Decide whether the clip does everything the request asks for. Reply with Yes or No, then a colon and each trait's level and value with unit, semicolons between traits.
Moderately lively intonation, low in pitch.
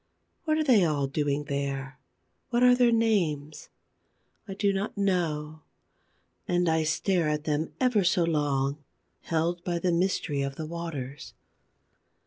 No: average, 4.7 semitones; medium, 165 Hz